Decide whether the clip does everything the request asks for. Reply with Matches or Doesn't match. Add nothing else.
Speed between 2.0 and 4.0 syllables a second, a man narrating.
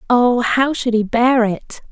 Doesn't match